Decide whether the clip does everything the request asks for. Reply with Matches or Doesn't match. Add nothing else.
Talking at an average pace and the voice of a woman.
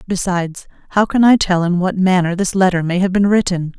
Doesn't match